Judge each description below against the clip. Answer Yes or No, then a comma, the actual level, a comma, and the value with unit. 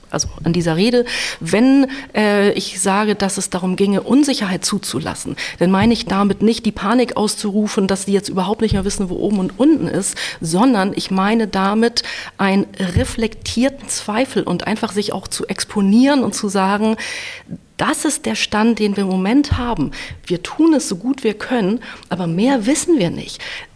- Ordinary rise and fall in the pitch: Yes, average, 3.8 semitones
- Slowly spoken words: No, average, 180 wpm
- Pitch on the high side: Yes, high, 210 Hz